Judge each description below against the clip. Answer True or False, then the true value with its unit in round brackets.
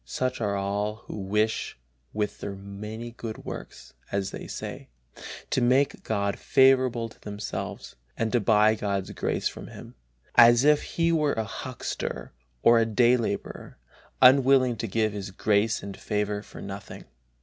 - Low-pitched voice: True (110 Hz)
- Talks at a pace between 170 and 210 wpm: False (155 wpm)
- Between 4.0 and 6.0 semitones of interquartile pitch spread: False (3.1 semitones)